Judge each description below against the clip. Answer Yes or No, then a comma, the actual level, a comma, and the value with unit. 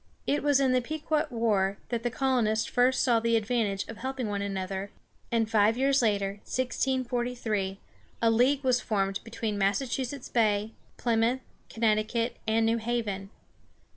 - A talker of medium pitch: No, high, 230 Hz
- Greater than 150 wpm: No, average, 145 wpm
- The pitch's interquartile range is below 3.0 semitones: No, average, 3.3 semitones